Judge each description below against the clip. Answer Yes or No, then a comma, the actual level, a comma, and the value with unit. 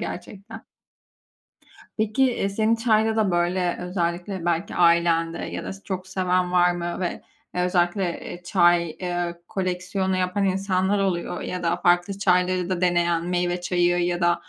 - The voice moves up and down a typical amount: No, narrow, 1.5 semitones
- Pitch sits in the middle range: Yes, medium, 180 Hz